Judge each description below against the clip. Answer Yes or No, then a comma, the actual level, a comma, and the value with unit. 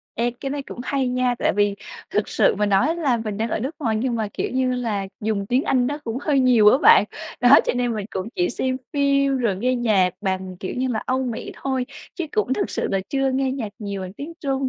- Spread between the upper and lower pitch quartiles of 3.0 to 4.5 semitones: Yes, average, 4.2 semitones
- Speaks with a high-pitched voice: Yes, high, 245 Hz